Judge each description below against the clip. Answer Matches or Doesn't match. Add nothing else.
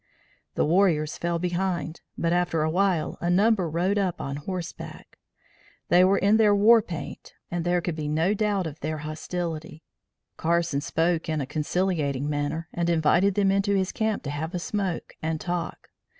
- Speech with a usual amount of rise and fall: Matches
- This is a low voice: Doesn't match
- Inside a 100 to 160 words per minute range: Doesn't match